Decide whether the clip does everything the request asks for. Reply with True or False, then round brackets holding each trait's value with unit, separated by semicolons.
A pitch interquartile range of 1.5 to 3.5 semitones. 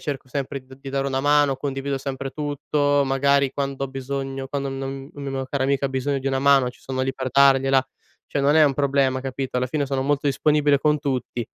False (1.0 semitones)